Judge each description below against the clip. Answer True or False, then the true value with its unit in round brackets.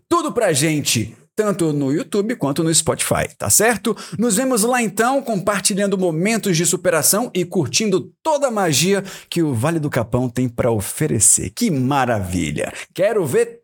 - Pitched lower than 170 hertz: False (190 Hz)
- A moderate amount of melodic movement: False (6.7 semitones)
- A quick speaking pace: False (160 wpm)